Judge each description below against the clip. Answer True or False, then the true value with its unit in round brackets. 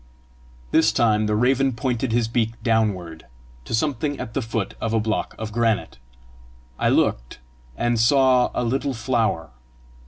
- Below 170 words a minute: True (150 wpm)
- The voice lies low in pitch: True (115 Hz)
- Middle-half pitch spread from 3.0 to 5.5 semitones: False (2.6 semitones)